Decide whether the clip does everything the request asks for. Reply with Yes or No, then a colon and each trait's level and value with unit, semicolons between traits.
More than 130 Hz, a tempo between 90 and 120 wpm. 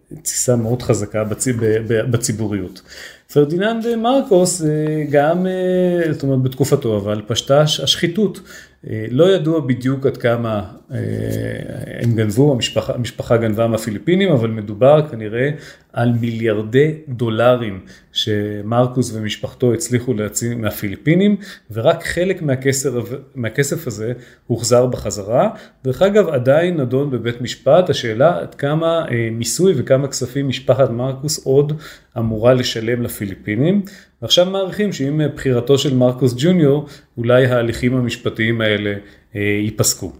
No: low, 125 Hz; average, 110 wpm